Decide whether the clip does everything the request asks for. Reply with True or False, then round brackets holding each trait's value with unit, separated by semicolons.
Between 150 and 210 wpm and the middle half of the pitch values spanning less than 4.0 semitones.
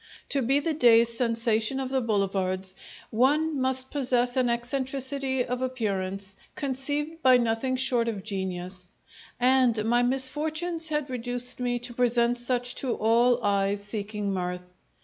False (140 wpm; 3.4 semitones)